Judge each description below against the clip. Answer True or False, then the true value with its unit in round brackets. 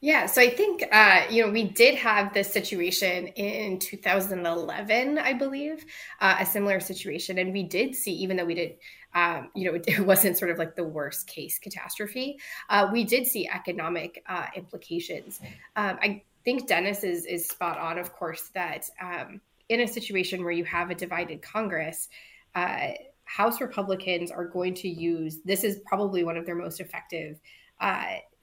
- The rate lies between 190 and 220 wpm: False (175 wpm)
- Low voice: False (190 Hz)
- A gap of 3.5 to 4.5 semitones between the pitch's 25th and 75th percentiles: True (4.0 semitones)